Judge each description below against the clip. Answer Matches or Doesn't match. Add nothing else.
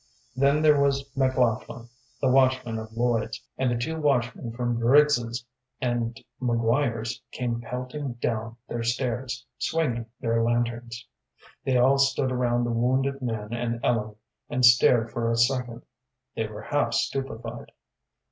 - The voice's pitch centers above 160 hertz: Doesn't match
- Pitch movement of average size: Doesn't match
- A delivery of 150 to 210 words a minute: Doesn't match